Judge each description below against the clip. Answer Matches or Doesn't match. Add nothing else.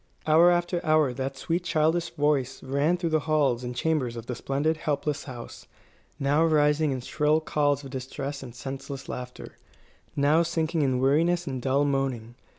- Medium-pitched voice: Matches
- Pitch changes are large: Doesn't match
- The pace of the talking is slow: Doesn't match